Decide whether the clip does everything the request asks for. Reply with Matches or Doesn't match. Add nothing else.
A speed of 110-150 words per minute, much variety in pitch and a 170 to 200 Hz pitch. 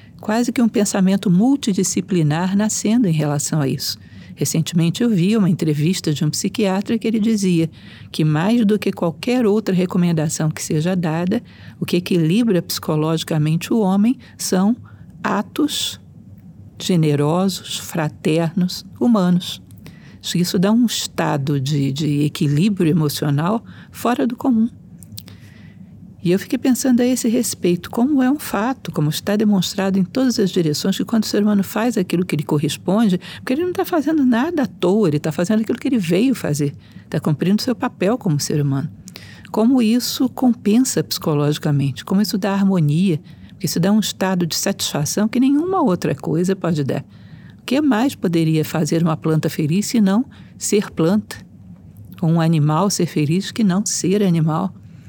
Doesn't match